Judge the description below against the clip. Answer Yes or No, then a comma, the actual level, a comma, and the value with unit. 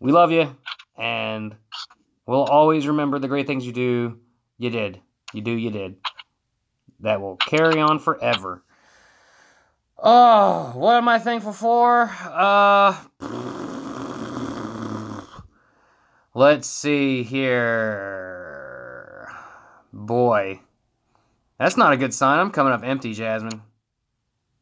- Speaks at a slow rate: Yes, slow, 105 wpm